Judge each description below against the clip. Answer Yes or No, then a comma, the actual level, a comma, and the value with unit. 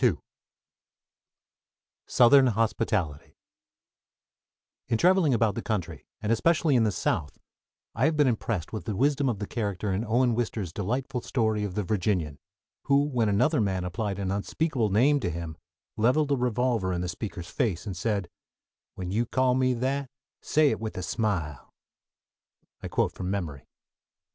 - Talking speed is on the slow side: No, average, 160 wpm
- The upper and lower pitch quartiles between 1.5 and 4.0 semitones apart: No, average, 5.2 semitones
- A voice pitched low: Yes, low, 110 Hz